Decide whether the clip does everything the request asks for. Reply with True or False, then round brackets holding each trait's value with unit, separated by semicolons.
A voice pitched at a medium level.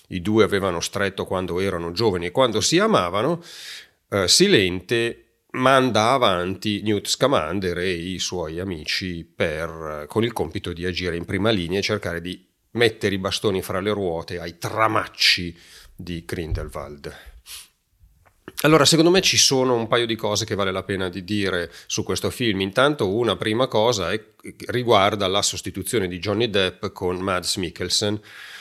False (100 Hz)